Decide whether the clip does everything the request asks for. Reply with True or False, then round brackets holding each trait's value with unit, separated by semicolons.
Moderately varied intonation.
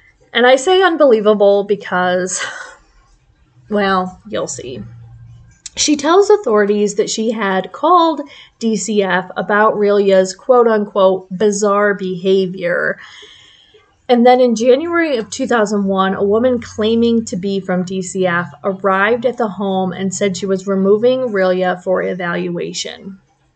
True (4.0 semitones)